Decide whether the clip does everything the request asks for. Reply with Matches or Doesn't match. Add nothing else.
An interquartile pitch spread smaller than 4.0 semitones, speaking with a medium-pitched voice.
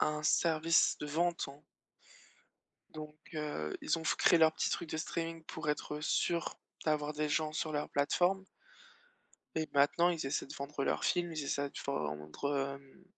Matches